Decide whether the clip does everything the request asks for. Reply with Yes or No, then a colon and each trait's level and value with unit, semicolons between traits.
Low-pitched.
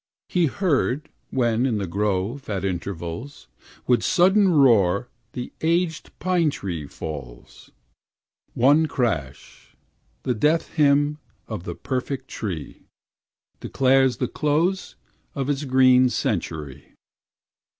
Yes: low, 130 Hz